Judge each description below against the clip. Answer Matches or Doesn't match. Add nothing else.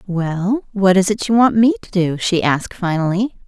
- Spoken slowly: Doesn't match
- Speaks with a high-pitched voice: Matches